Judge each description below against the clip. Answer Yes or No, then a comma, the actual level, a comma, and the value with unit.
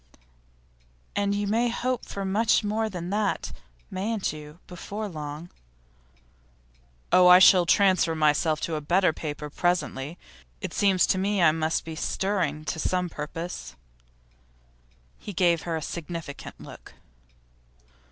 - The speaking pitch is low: No, medium, 180 Hz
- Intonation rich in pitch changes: No, average, 4.1 semitones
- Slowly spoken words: Yes, slow, 130 wpm